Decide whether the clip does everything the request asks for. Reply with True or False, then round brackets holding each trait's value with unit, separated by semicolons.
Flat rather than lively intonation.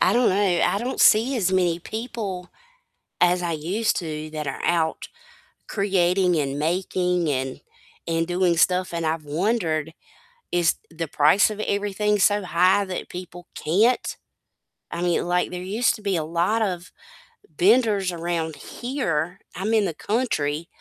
False (3.7 semitones)